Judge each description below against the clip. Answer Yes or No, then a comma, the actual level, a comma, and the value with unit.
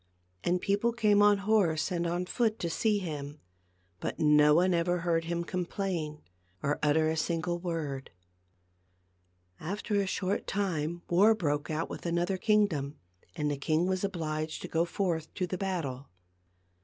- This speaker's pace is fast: No, average, 160 wpm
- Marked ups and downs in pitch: No, average, 3.8 semitones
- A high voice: No, medium, 170 Hz